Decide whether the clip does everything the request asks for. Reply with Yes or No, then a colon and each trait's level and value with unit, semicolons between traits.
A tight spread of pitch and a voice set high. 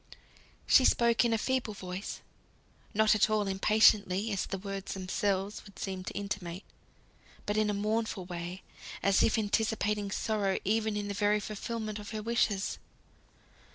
Yes: narrow, 1.9 semitones; high, 205 Hz